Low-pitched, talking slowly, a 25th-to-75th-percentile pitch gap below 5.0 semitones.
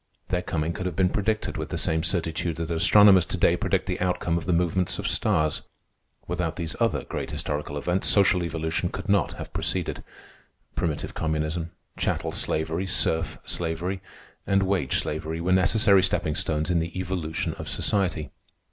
No: very low, 85 Hz; average, 165 wpm; narrow, 2.6 semitones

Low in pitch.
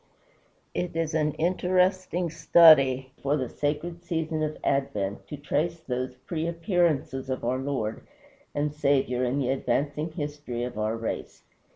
No: medium, 145 Hz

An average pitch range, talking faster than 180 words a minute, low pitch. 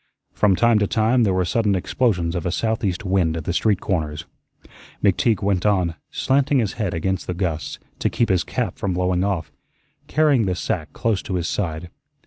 Yes: average, 3.8 semitones; average, 190 wpm; very low, 95 Hz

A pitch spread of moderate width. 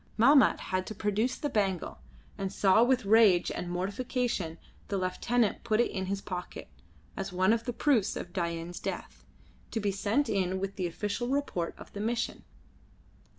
Yes: average, 3.9 semitones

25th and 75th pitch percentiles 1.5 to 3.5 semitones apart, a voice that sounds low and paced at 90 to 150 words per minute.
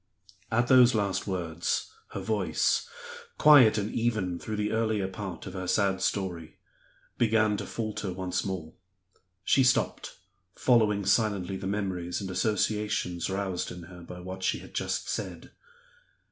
Yes: average, 3.0 semitones; low, 100 Hz; average, 145 wpm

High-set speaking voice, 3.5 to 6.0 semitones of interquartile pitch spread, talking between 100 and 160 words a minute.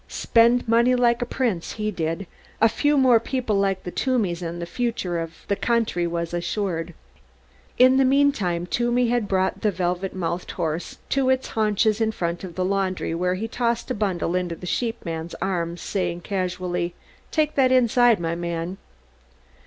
No: high, 195 Hz; wide, 5.4 semitones; average, 170 wpm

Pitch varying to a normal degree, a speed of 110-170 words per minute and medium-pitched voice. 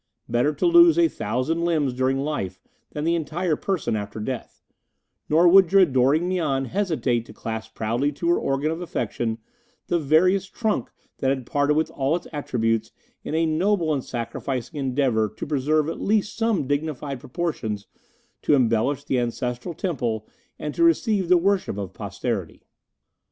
No: wide, 5.8 semitones; average, 160 wpm; medium, 145 Hz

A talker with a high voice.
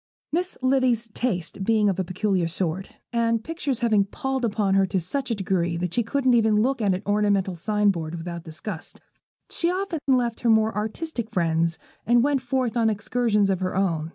Yes: high, 215 Hz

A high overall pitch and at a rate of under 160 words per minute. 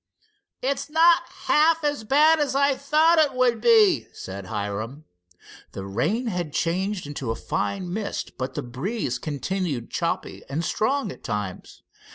Yes: high, 200 Hz; average, 150 wpm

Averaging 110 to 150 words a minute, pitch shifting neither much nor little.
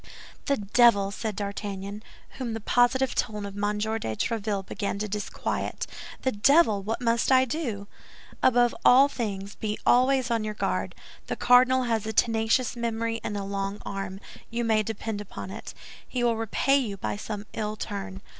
No: average, 170 wpm; average, 3.0 semitones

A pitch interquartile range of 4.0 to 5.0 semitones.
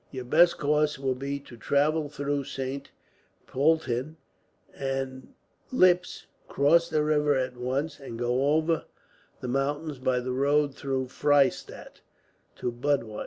No: narrow, 2.4 semitones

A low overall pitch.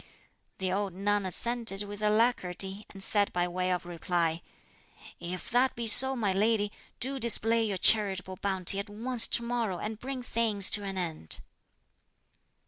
No: high, 205 Hz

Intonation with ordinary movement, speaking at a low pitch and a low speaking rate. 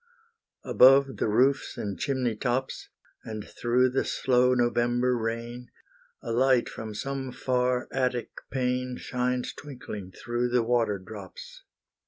No: narrow, 1.5 semitones; low, 125 Hz; slow, 125 wpm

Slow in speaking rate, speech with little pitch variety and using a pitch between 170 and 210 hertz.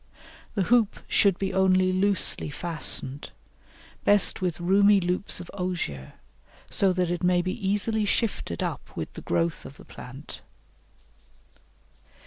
Yes: slow, 130 wpm; narrow, 2.3 semitones; medium, 185 Hz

